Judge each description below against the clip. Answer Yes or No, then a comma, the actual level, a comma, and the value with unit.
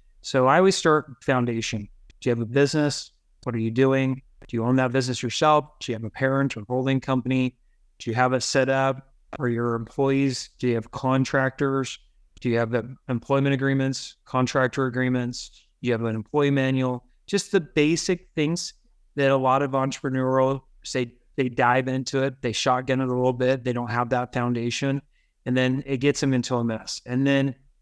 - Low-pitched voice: Yes, low, 130 Hz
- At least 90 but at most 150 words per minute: No, average, 190 wpm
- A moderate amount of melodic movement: No, narrow, 1.9 semitones